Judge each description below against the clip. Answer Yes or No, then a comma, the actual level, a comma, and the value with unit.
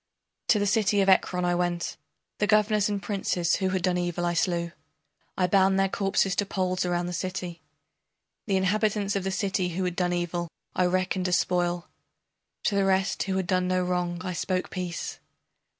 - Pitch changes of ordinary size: No, narrow, 1.6 semitones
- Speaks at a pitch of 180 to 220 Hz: Yes, medium, 185 Hz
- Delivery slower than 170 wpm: No, average, 190 wpm